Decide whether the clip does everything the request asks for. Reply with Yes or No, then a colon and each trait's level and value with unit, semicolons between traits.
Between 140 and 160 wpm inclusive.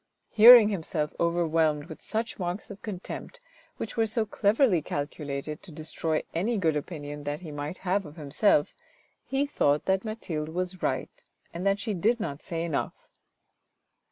Yes: average, 155 wpm